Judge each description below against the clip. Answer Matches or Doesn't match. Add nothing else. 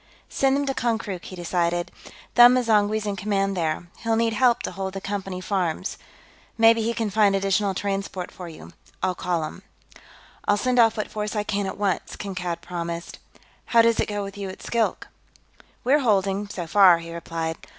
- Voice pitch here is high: Matches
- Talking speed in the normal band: Matches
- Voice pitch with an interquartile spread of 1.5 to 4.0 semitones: Matches